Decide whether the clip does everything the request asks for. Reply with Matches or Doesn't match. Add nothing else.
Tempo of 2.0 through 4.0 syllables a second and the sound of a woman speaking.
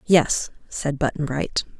Matches